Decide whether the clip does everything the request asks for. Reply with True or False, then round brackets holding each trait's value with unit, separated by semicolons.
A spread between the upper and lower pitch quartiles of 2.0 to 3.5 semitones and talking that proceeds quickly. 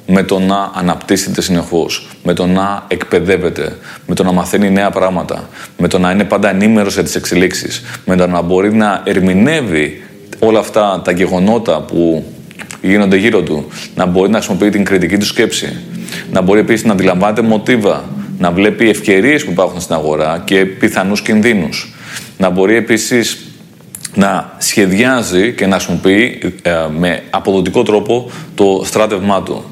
False (2.4 semitones; 155 wpm)